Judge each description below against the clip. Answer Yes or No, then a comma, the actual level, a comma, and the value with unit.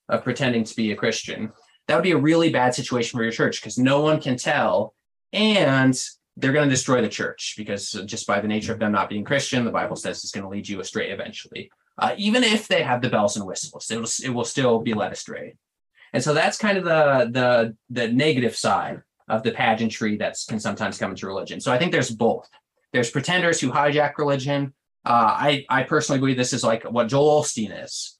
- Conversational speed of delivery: No, fast, 225 wpm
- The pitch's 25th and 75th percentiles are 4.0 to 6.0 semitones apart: Yes, average, 4.6 semitones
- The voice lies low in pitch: Yes, low, 130 Hz